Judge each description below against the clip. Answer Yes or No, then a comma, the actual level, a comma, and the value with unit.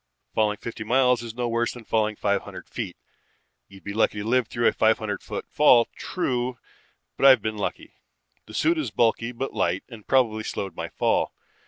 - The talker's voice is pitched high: No, low, 115 Hz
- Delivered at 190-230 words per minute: Yes, average, 195 wpm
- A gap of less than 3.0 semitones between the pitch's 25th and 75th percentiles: Yes, narrow, 2.6 semitones